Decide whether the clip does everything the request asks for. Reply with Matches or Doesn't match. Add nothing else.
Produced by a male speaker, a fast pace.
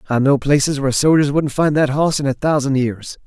Matches